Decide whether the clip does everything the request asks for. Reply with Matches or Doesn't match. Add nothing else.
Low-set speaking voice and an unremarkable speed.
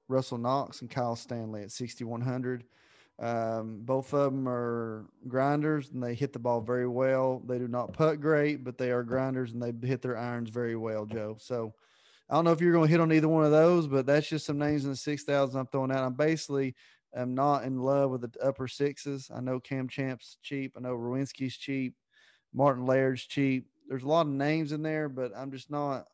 Doesn't match